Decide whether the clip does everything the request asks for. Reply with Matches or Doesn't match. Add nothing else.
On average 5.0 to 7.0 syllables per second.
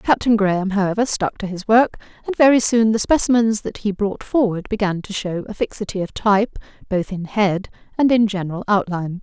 Matches